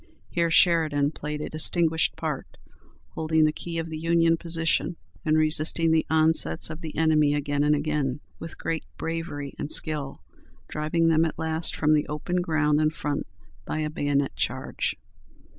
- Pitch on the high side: No, medium, 155 Hz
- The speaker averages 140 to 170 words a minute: Yes, average, 160 wpm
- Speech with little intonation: Yes, narrow, 1.6 semitones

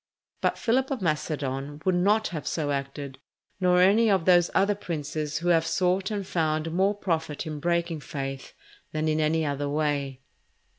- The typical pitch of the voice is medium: Yes, medium, 160 Hz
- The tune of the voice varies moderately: Yes, average, 3.9 semitones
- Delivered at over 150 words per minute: Yes, average, 165 wpm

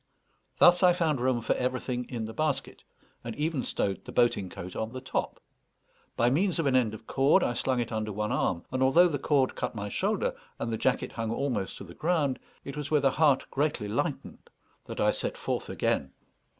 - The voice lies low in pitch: Yes, low, 130 Hz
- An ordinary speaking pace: No, fast, 210 wpm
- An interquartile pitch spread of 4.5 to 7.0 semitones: Yes, average, 4.9 semitones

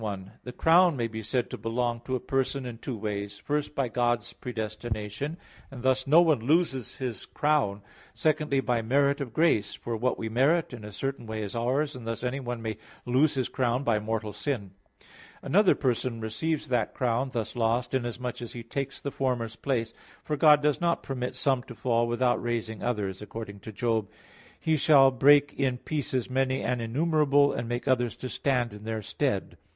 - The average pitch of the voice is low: Yes, low, 125 Hz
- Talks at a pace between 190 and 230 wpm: Yes, average, 195 wpm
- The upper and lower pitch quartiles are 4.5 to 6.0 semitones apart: No, average, 3.4 semitones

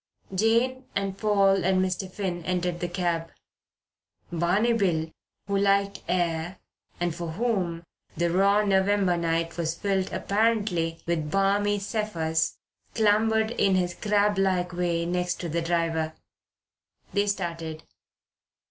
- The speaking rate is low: Yes, slow, 120 wpm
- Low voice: No, medium, 185 Hz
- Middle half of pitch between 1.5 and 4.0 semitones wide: Yes, average, 3.0 semitones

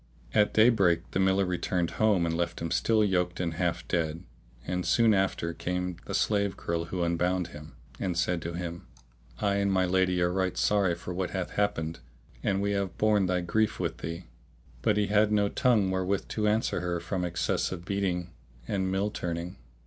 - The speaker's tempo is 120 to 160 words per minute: No, average, 195 wpm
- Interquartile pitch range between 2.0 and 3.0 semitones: Yes, narrow, 2.6 semitones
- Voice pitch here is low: Yes, very low, 90 Hz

